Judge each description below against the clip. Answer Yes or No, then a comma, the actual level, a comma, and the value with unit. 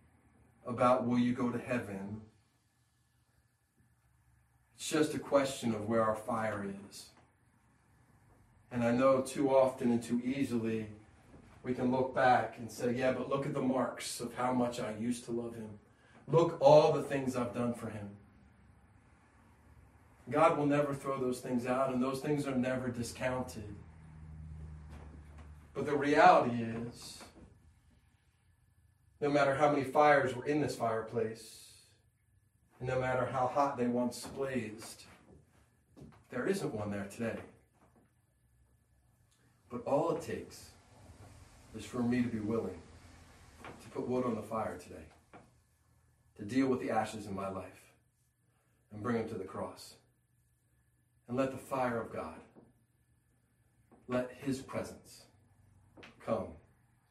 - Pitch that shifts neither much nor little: Yes, average, 3.0 semitones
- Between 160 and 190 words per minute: No, average, 140 wpm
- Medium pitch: No, low, 115 Hz